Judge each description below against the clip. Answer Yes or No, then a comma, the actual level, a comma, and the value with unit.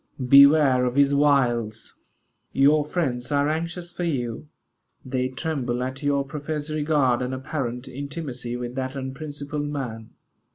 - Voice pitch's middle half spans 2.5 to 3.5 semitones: Yes, average, 2.9 semitones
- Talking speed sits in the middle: No, slow, 130 wpm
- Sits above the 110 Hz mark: Yes, medium, 140 Hz